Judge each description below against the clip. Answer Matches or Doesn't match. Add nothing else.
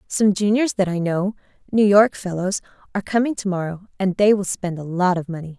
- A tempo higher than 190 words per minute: Matches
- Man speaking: Doesn't match